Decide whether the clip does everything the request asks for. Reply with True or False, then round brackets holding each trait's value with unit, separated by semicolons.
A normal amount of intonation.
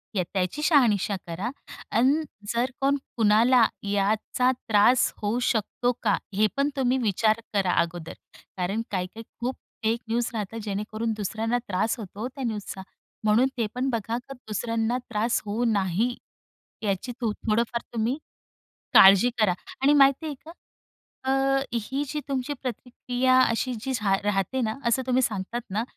True (3.4 semitones)